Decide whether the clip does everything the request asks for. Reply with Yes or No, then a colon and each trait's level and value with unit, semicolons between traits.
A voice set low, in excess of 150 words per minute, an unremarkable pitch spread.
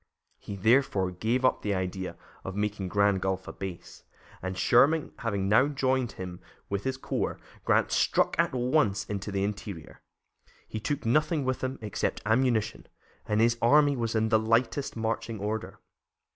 Yes: low, 110 Hz; average, 160 wpm; average, 4.5 semitones